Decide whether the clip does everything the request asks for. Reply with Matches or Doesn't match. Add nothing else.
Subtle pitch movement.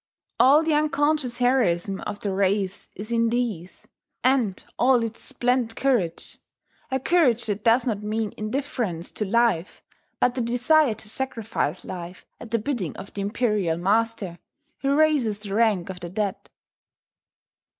Doesn't match